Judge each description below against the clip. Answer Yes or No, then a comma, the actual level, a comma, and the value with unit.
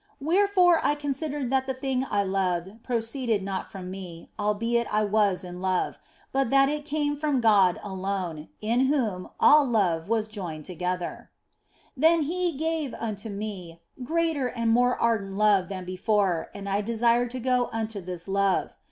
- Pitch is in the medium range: No, high, 220 Hz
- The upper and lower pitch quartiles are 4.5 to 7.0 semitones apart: Yes, wide, 5.6 semitones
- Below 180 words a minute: Yes, average, 160 wpm